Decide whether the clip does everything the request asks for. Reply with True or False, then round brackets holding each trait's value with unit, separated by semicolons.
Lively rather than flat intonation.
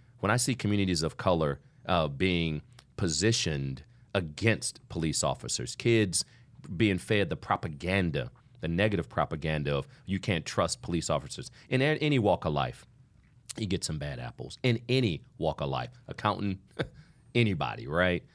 True (6.5 semitones)